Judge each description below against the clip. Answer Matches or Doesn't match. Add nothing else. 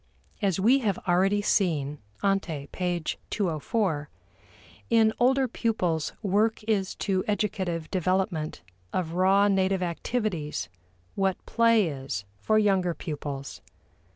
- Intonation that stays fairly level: Doesn't match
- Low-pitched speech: Doesn't match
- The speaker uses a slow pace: Matches